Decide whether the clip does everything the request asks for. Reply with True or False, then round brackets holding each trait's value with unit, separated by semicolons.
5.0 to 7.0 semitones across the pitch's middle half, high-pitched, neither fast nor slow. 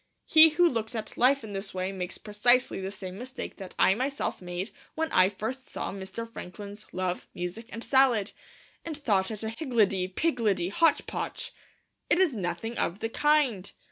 True (5.4 semitones; 220 Hz; 175 wpm)